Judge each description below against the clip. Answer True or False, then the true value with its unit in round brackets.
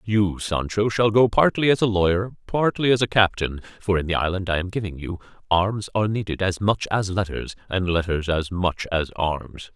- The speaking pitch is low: True (95 Hz)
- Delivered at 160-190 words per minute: False (205 wpm)